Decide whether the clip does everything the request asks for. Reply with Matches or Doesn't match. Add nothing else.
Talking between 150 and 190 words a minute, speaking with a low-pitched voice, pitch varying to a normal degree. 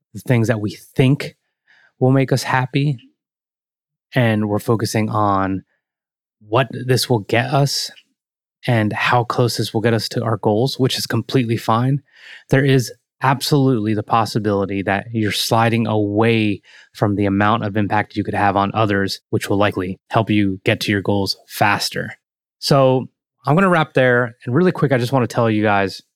Matches